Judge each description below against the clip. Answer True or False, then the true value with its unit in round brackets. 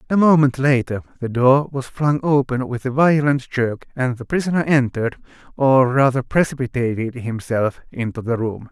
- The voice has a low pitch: True (130 Hz)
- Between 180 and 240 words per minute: False (160 wpm)